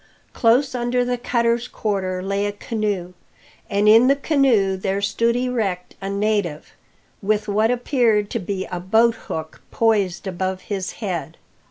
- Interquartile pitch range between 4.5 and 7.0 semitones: No, average, 3.6 semitones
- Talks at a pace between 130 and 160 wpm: Yes, average, 145 wpm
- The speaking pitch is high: Yes, high, 210 Hz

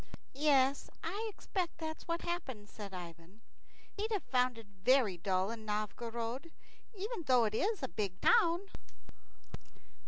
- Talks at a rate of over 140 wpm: No, slow, 135 wpm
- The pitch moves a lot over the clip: Yes, wide, 8.3 semitones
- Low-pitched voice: No, very high, 255 Hz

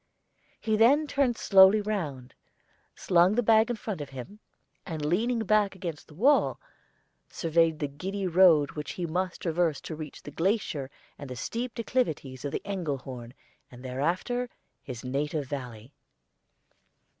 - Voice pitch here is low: No, medium, 170 Hz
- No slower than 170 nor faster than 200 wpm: No, average, 145 wpm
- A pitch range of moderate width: No, wide, 6.9 semitones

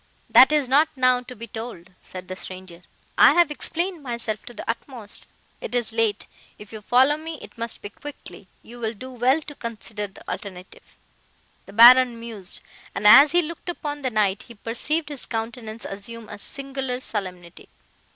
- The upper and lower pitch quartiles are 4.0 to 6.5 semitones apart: Yes, average, 4.4 semitones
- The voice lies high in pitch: Yes, high, 235 Hz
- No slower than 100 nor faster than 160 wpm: No, average, 175 wpm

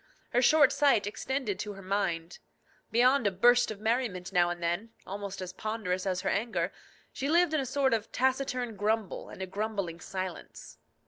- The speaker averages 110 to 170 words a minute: No, average, 180 wpm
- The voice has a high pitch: Yes, high, 210 Hz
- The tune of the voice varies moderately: Yes, average, 5.0 semitones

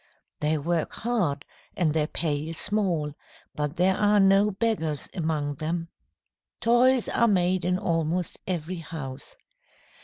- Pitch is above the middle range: No, medium, 170 Hz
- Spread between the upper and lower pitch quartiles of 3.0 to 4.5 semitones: Yes, average, 4.2 semitones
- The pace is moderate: No, slow, 130 wpm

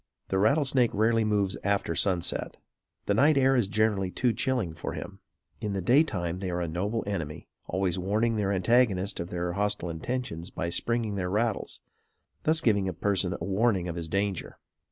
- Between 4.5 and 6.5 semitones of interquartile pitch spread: No, average, 4.1 semitones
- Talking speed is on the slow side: No, average, 175 wpm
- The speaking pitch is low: Yes, low, 100 Hz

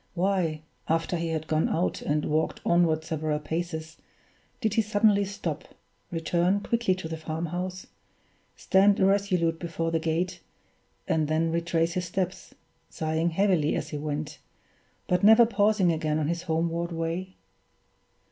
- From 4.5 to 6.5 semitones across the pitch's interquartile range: No, average, 2.8 semitones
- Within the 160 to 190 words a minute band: No, average, 145 wpm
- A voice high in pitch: No, medium, 170 Hz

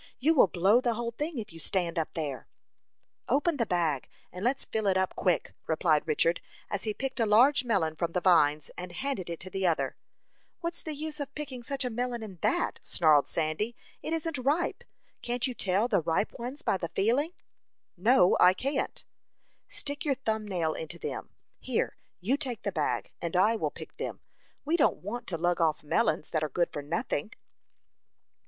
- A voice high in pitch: Yes, high, 205 Hz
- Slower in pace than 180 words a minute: No, average, 195 wpm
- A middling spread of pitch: No, wide, 7.3 semitones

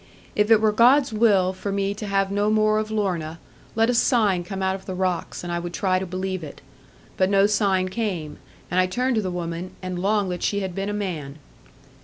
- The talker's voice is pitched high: Yes, high, 195 Hz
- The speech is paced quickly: Yes, fast, 230 wpm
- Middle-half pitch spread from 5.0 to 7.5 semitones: No, narrow, 2.5 semitones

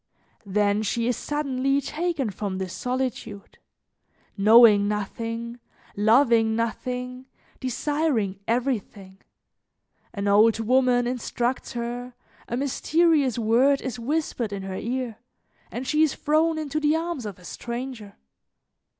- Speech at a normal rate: No, slow, 115 wpm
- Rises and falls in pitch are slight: No, average, 3.9 semitones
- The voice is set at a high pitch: Yes, high, 240 Hz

